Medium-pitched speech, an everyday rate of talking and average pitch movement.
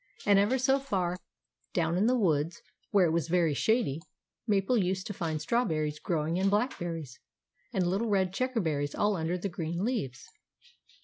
Yes: medium, 180 Hz; average, 165 wpm; average, 4.2 semitones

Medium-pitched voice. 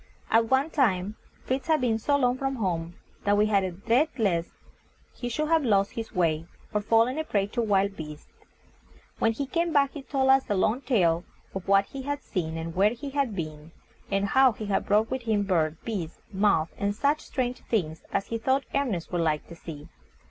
No: high, 215 Hz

